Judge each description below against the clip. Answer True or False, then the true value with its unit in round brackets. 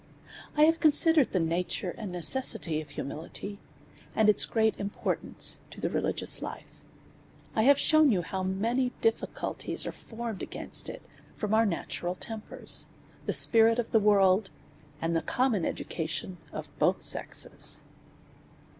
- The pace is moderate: True (145 wpm)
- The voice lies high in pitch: True (210 Hz)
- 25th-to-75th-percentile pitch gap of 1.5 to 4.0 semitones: False (4.7 semitones)